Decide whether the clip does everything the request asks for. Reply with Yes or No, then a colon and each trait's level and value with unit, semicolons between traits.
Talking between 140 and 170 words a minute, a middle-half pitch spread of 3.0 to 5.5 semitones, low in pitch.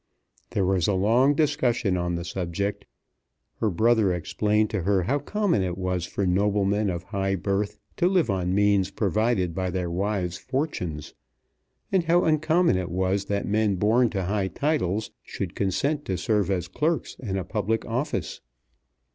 Yes: average, 165 wpm; average, 4.0 semitones; low, 100 Hz